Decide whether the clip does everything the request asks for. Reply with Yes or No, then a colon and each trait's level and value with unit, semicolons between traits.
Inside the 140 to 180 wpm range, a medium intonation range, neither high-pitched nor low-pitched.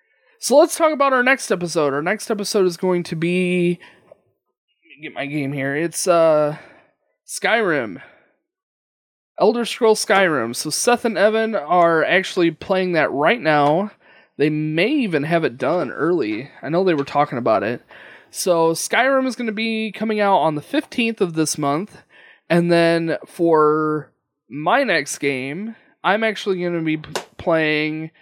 No: average, 165 wpm; wide, 6.0 semitones; medium, 175 Hz